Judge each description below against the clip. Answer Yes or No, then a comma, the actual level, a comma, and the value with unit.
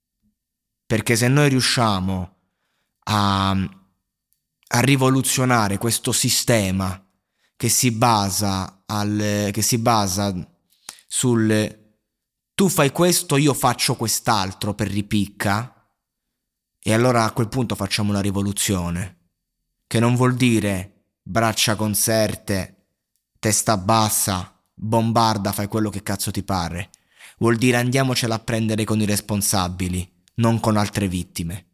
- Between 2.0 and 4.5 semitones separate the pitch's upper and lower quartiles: Yes, average, 3.2 semitones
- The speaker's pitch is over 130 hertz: No, low, 105 Hz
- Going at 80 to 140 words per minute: Yes, slow, 115 wpm